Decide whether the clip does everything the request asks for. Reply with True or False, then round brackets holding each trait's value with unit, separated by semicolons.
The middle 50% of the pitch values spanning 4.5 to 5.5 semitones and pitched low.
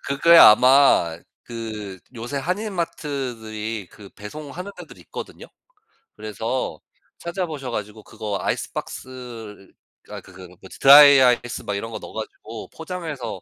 True (5.1 semitones; 120 Hz)